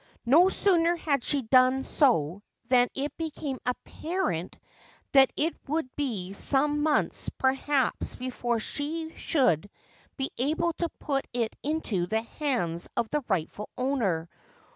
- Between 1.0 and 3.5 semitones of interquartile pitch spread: No, average, 4.8 semitones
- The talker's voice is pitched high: Yes, very high, 265 Hz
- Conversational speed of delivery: No, slow, 130 wpm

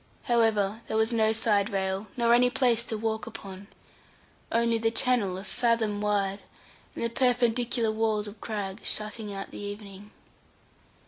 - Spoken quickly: No, average, 150 wpm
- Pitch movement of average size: No, narrow, 2.2 semitones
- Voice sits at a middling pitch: No, high, 220 Hz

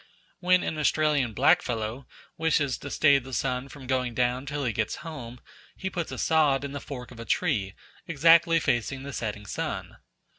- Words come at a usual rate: Yes, average, 180 wpm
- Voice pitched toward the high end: No, low, 135 Hz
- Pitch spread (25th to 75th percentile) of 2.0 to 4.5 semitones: Yes, average, 4.0 semitones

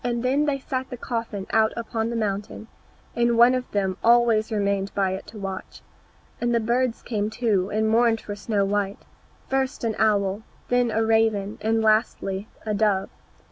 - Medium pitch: No, high, 220 Hz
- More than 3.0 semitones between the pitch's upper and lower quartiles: No, average, 2.7 semitones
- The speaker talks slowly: No, average, 175 wpm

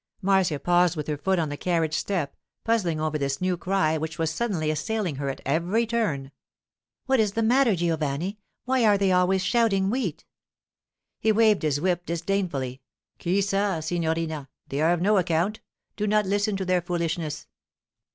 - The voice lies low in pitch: No, medium, 180 Hz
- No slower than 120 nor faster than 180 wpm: Yes, average, 170 wpm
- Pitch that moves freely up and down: No, average, 4.4 semitones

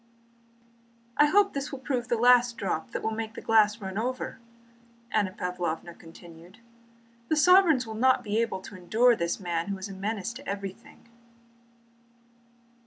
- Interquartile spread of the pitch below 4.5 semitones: No, average, 4.8 semitones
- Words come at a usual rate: Yes, average, 160 wpm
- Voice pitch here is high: Yes, high, 220 Hz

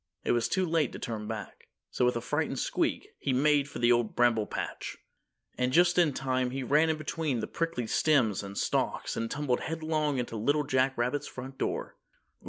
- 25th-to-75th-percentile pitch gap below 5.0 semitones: Yes, average, 4.2 semitones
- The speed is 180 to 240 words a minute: Yes, average, 195 wpm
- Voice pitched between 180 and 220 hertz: No, low, 130 Hz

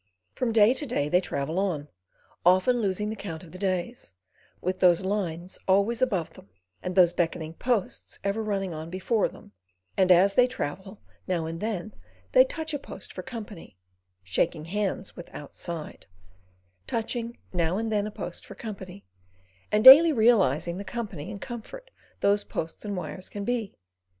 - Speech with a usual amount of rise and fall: Yes, average, 4.4 semitones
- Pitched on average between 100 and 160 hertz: No, high, 195 Hz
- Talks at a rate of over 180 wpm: No, average, 165 wpm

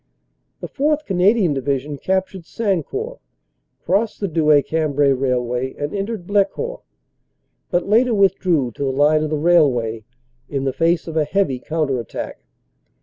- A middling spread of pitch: No, wide, 6.2 semitones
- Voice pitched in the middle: Yes, medium, 160 Hz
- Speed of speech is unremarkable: Yes, average, 145 wpm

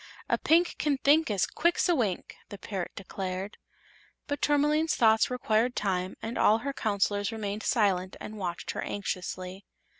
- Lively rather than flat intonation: Yes, wide, 6.2 semitones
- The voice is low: No, high, 215 Hz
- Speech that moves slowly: No, average, 155 wpm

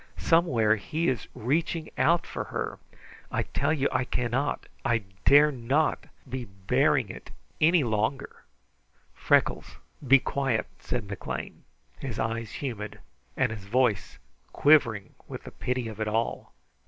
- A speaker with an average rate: No, slow, 130 wpm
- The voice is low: Yes, low, 125 Hz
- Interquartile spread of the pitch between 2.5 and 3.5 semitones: No, average, 4.4 semitones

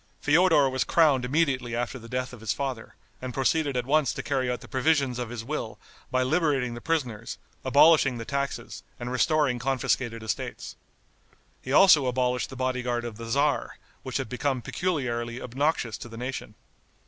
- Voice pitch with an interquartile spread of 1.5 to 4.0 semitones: Yes, average, 2.9 semitones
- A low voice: Yes, low, 130 Hz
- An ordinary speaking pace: Yes, average, 175 wpm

